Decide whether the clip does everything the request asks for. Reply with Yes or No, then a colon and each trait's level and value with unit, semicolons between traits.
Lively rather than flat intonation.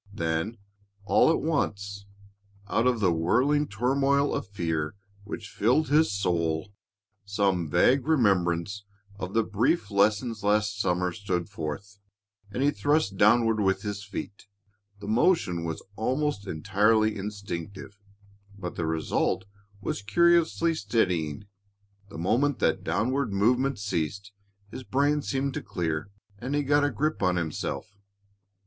Yes: wide, 5.7 semitones